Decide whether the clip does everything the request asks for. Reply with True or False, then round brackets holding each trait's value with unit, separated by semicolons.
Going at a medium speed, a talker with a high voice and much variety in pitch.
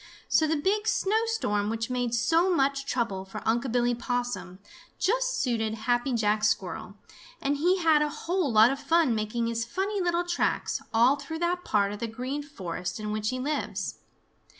True (175 wpm; 250 Hz; 6.7 semitones)